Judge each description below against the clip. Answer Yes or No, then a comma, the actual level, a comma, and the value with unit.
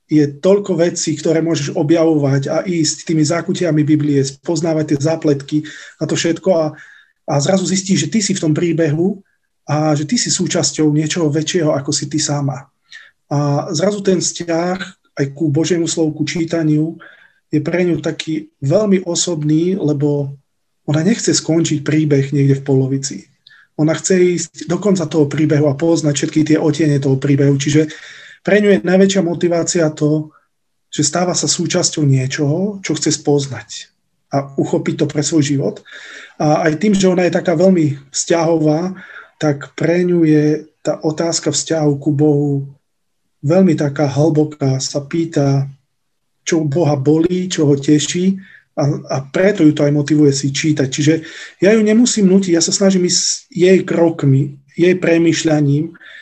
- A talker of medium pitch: Yes, medium, 155 Hz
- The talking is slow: No, average, 160 wpm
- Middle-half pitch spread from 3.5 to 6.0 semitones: No, narrow, 2.6 semitones